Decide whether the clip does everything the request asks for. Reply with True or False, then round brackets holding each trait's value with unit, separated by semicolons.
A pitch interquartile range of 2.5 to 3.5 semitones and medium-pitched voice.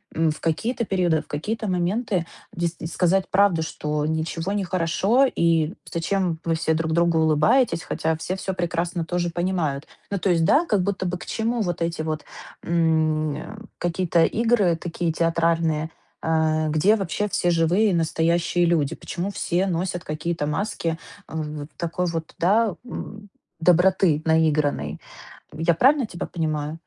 True (2.8 semitones; 170 Hz)